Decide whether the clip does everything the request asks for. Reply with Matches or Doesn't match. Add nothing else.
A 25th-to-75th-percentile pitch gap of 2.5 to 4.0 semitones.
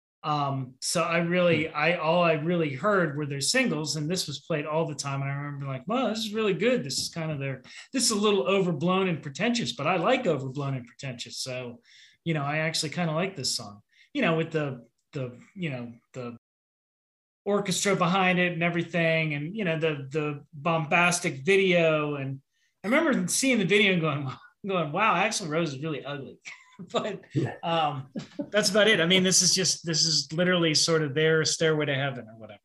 Doesn't match